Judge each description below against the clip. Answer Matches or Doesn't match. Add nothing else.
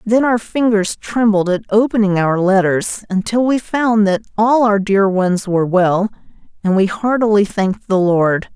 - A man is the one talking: Doesn't match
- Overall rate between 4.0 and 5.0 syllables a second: Matches